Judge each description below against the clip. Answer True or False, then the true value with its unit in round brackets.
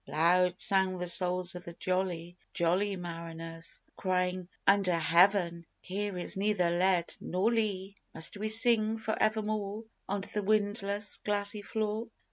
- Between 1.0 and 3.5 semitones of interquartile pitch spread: True (2.8 semitones)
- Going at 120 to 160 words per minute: True (135 wpm)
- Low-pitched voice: False (190 Hz)